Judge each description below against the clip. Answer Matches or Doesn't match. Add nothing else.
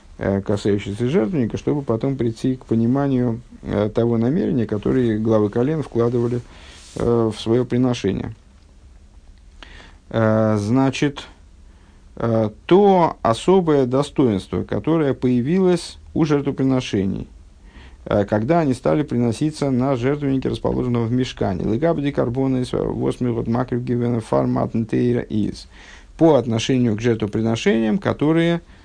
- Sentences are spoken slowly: Matches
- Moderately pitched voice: Doesn't match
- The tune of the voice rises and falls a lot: Doesn't match